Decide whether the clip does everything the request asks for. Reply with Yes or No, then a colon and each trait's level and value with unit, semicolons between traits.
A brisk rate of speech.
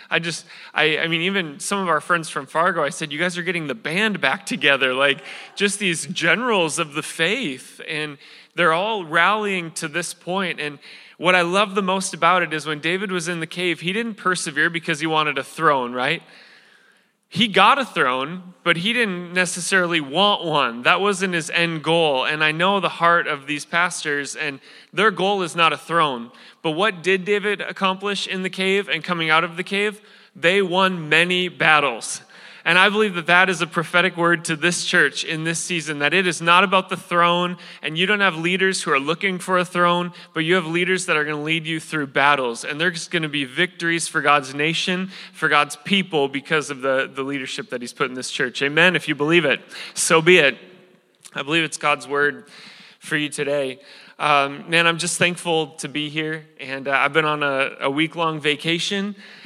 Yes: fast, 210 wpm